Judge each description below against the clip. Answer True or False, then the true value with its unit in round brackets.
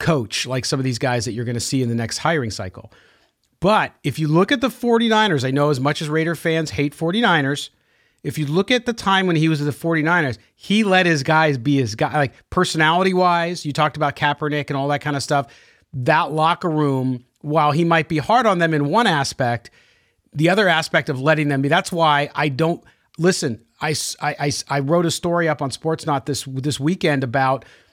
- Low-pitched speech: False (150 Hz)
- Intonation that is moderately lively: True (3.2 semitones)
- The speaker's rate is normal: False (220 wpm)